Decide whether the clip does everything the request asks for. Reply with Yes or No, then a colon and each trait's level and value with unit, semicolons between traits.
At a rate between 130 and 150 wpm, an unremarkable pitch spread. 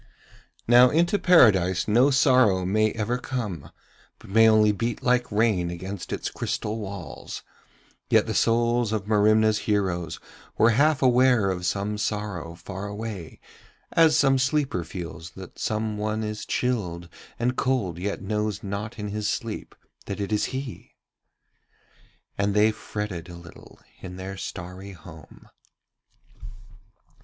Yes: slow, 135 wpm; average, 3.8 semitones